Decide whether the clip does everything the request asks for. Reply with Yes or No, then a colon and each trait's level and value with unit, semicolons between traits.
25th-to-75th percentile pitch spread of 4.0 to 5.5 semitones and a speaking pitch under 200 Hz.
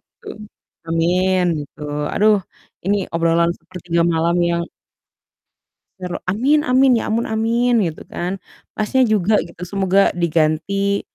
Yes: average, 4.3 semitones; high, 190 Hz